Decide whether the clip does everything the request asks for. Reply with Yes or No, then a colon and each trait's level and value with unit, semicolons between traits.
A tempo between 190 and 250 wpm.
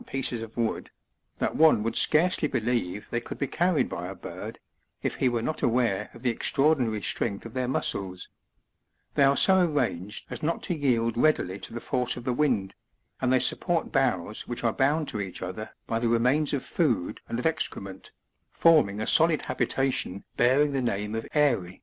Yes: average, 195 wpm